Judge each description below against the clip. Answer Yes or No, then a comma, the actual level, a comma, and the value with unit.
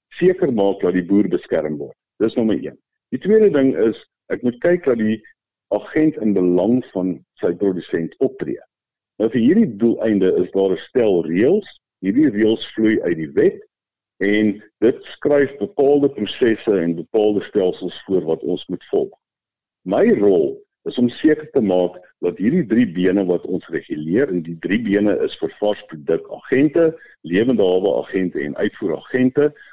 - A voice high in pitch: No, low, 125 Hz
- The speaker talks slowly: No, average, 160 wpm